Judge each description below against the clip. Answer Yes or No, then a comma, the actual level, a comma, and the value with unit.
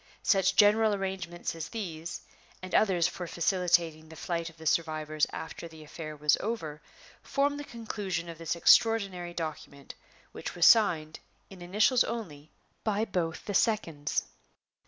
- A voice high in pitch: No, medium, 175 Hz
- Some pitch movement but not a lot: Yes, average, 4.2 semitones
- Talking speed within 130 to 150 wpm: Yes, average, 145 wpm